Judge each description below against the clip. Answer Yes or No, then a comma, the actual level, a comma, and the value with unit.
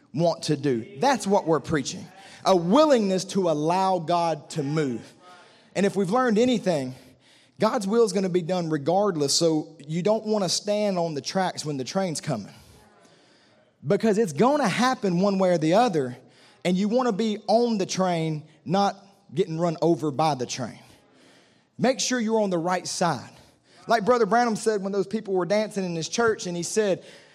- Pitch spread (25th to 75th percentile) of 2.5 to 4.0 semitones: No, average, 4.8 semitones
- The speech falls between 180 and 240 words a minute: Yes, average, 190 wpm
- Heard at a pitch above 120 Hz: Yes, medium, 185 Hz